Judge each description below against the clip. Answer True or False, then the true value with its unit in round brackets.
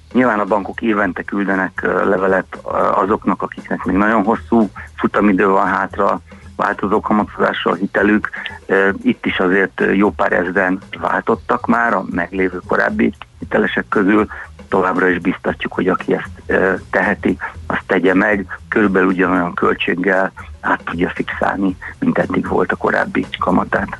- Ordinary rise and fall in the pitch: False (1.6 semitones)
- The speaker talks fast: False (130 wpm)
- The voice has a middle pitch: False (95 Hz)